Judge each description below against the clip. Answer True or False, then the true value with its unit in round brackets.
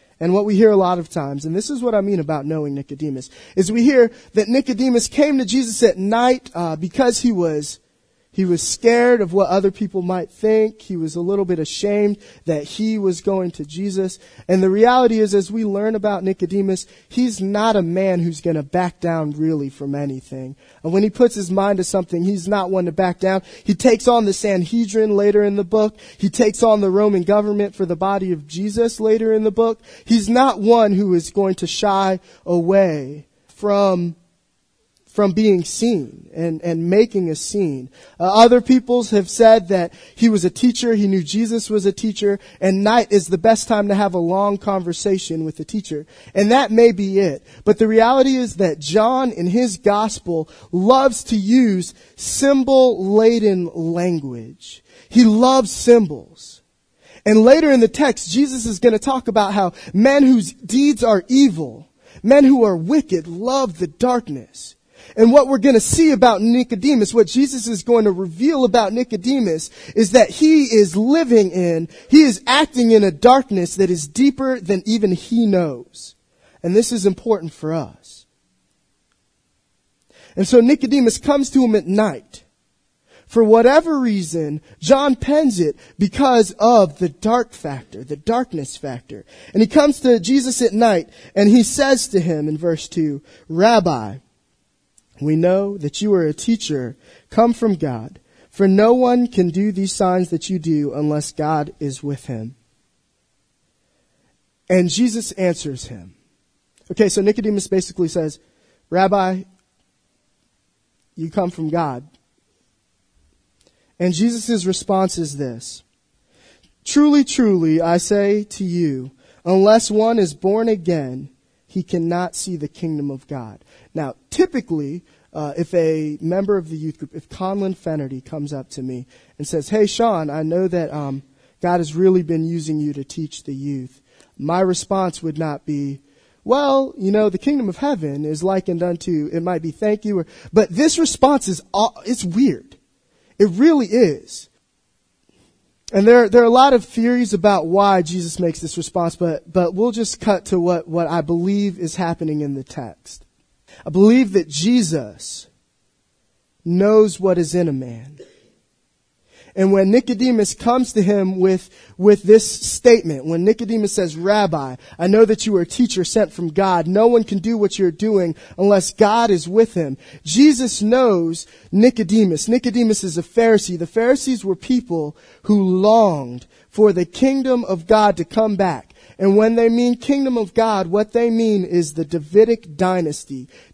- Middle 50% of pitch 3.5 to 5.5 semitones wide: True (5.2 semitones)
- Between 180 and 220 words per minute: False (170 wpm)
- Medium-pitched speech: False (195 Hz)